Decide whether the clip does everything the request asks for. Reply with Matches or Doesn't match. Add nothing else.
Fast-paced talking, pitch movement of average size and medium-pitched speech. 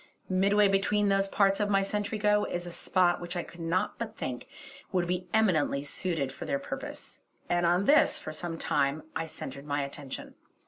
Doesn't match